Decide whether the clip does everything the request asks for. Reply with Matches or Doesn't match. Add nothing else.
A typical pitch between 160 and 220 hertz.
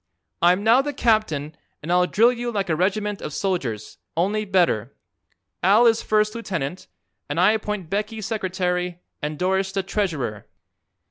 Matches